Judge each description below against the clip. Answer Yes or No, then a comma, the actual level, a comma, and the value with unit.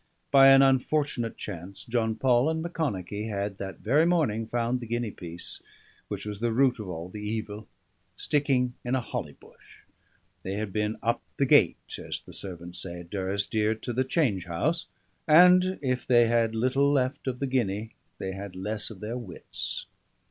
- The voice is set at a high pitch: No, low, 115 Hz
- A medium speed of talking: Yes, average, 175 wpm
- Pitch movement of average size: Yes, average, 4.6 semitones